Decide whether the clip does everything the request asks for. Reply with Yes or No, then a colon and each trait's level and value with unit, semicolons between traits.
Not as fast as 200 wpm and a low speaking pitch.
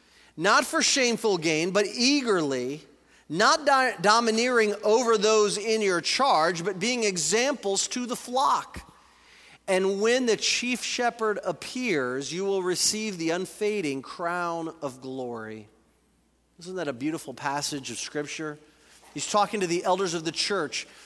No: average, 140 wpm; high, 195 Hz